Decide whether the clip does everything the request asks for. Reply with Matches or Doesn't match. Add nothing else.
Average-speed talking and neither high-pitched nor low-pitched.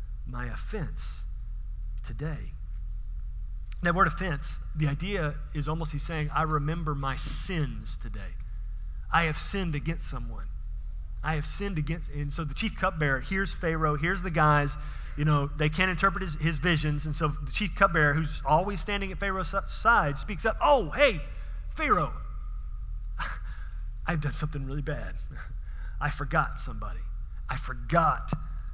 Matches